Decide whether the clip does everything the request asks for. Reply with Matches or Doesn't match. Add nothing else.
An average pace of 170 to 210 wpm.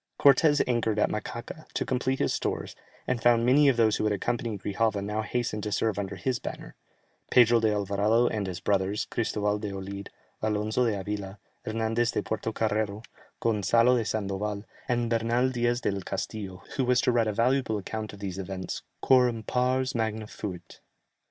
Matches